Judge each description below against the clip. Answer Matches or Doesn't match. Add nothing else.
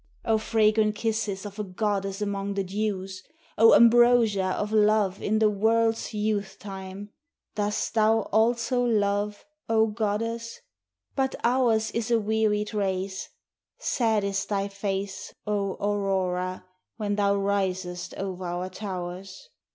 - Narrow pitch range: Matches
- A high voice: Matches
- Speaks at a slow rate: Matches